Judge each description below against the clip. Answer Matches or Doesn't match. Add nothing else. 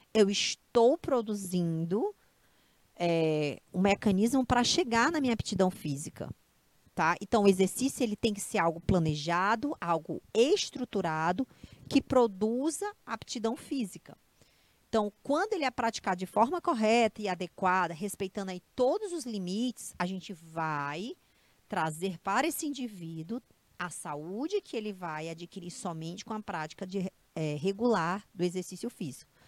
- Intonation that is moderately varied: Doesn't match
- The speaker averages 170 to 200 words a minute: Doesn't match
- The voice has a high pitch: Matches